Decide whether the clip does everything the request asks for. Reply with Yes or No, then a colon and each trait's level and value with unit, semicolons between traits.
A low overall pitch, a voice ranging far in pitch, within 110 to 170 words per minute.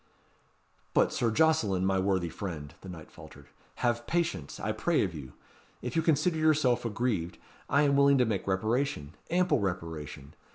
Yes: low, 110 Hz; wide, 8.0 semitones; average, 160 wpm